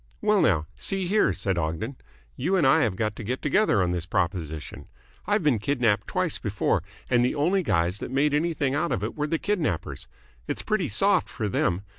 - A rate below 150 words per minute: No, average, 200 wpm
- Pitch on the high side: No, low, 130 Hz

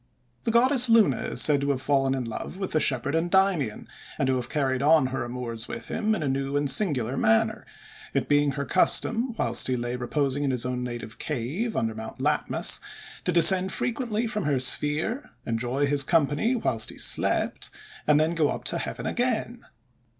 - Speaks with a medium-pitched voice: Yes, medium, 145 Hz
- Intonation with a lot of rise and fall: Yes, wide, 7.0 semitones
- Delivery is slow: No, average, 185 wpm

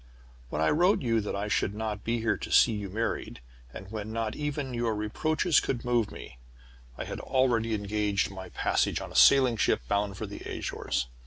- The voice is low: Yes, low, 110 Hz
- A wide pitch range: No, average, 3.1 semitones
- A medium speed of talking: Yes, average, 195 wpm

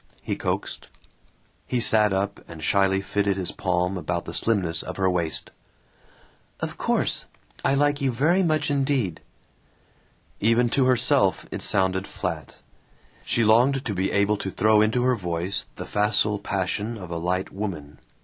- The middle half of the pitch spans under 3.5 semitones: No, average, 4.6 semitones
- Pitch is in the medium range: No, low, 100 Hz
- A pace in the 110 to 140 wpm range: No, average, 155 wpm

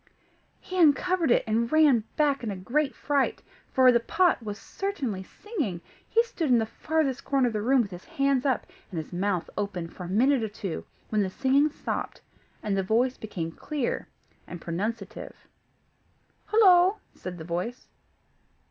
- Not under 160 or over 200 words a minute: Yes, average, 170 wpm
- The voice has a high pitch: Yes, high, 240 Hz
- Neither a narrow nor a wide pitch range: No, wide, 6.6 semitones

